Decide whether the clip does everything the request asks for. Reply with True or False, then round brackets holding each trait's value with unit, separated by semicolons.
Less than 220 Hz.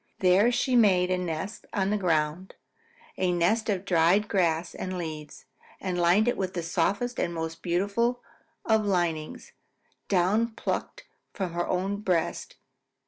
True (185 Hz)